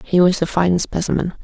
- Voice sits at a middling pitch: Yes, medium, 175 Hz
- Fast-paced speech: Yes, fast, 210 wpm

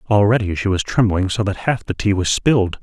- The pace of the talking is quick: Yes, fast, 235 wpm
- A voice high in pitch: No, low, 100 Hz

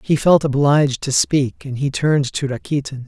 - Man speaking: Yes, male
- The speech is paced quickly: No, average, 195 wpm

